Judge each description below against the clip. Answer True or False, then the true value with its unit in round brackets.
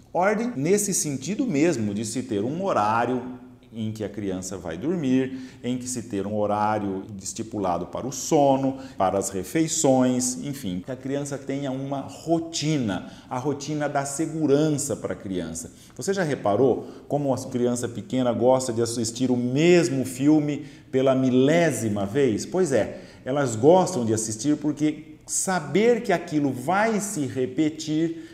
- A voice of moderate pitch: False (130 Hz)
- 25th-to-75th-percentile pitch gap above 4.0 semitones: True (5.0 semitones)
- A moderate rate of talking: True (150 wpm)